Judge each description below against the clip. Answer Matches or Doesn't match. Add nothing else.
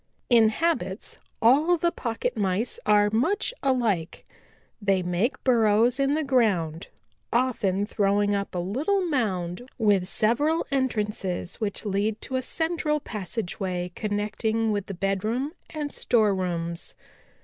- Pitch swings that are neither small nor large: Matches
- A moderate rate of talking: Doesn't match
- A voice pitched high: Matches